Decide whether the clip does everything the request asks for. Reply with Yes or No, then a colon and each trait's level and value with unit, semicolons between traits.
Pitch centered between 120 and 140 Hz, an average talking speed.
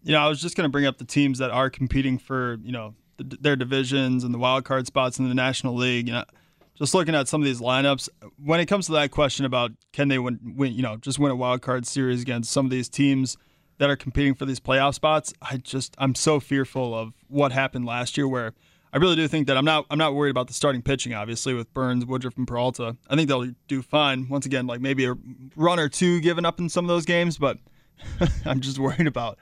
No: low, 135 Hz; fast, 255 wpm